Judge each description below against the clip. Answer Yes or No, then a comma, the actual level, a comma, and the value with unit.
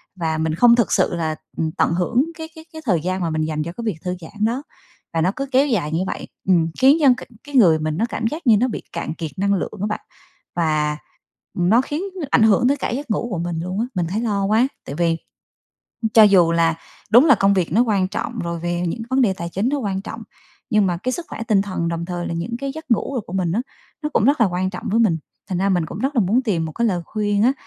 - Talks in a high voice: Yes, high, 195 Hz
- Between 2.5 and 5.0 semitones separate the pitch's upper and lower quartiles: No, wide, 5.6 semitones